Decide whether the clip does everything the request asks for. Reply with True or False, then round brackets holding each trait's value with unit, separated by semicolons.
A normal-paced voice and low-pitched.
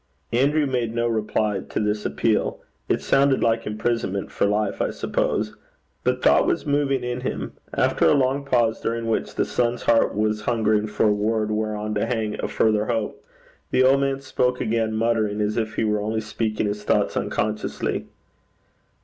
True (175 wpm; 110 Hz)